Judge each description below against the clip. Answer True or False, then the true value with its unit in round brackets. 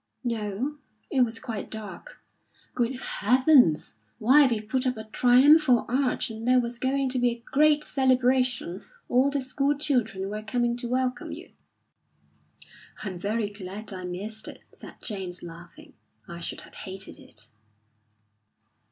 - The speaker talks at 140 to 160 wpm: True (145 wpm)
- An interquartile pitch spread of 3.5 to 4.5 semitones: True (4.1 semitones)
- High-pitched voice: True (240 Hz)